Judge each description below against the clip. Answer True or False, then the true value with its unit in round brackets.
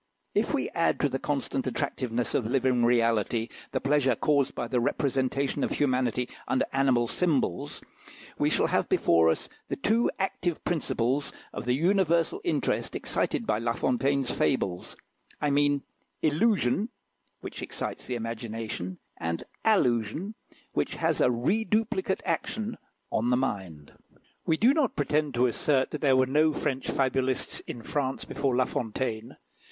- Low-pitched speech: True (130 Hz)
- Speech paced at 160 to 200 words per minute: False (145 wpm)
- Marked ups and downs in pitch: False (4.2 semitones)